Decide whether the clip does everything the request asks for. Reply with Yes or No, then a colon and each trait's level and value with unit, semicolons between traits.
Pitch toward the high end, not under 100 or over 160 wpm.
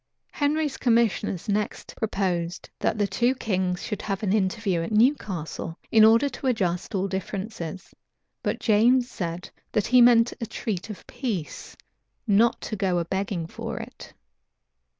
Yes: high, 205 Hz; average, 150 wpm